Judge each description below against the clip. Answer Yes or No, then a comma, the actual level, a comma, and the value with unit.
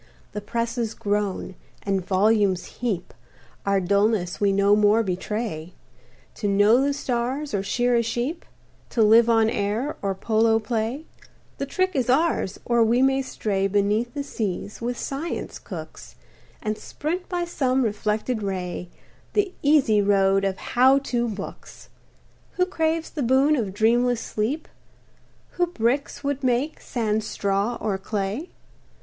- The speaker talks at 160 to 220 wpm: No, average, 145 wpm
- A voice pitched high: Yes, high, 225 Hz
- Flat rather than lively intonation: No, average, 4.5 semitones